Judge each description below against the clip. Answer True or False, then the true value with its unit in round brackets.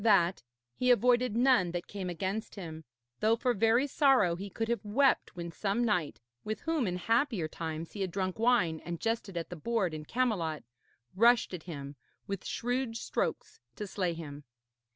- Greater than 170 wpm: True (180 wpm)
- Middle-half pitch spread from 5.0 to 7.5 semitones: True (5.5 semitones)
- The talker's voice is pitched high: True (200 Hz)